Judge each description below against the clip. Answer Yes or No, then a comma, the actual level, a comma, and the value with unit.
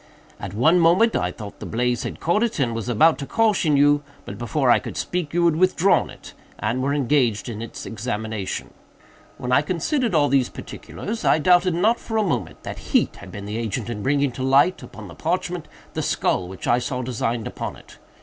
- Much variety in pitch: Yes, wide, 6.8 semitones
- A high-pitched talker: No, low, 135 Hz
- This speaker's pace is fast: Yes, fast, 210 wpm